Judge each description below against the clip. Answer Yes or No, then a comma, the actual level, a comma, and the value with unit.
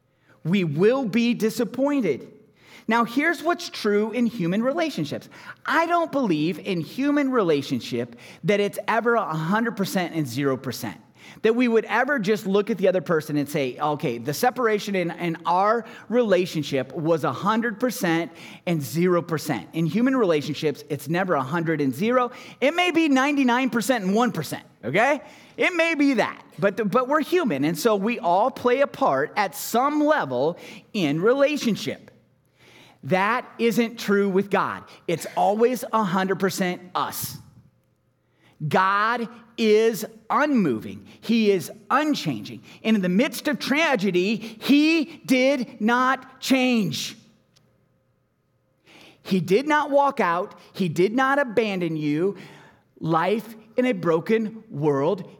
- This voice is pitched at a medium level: No, high, 215 Hz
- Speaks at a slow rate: Yes, slow, 130 wpm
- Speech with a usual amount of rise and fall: No, wide, 6.8 semitones